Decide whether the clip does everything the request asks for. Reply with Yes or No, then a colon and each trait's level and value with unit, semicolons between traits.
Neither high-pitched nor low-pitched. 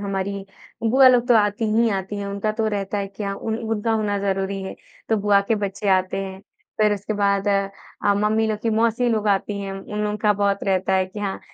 No: high, 205 Hz